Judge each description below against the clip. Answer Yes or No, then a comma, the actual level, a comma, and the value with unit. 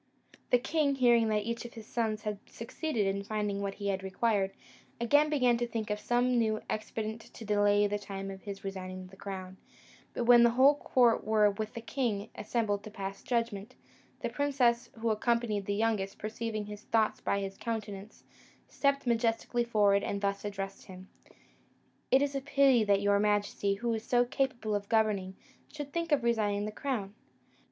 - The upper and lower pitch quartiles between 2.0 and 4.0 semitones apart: Yes, average, 2.9 semitones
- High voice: Yes, high, 215 Hz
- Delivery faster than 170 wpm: Yes, average, 180 wpm